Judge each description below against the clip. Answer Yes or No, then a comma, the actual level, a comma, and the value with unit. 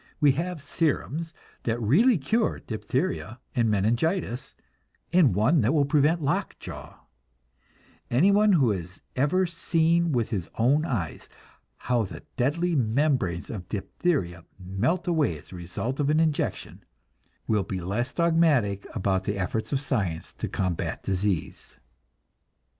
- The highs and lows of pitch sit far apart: Yes, wide, 8.2 semitones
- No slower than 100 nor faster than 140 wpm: Yes, slow, 135 wpm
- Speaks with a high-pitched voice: No, low, 130 Hz